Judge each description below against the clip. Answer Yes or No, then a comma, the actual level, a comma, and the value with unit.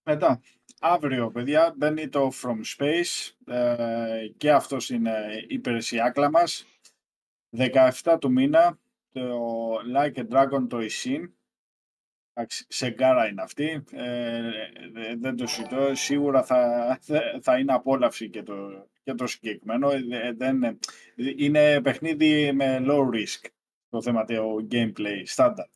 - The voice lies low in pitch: Yes, low, 130 Hz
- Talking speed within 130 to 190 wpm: No, average, 120 wpm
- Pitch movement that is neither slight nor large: Yes, average, 3.9 semitones